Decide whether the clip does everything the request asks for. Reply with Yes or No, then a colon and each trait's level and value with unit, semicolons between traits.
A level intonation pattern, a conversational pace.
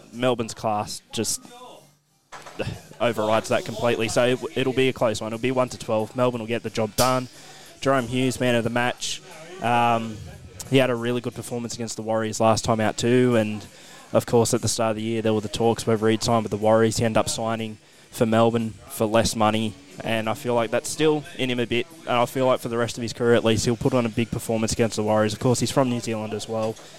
No: narrow, 1.9 semitones; fast, 250 wpm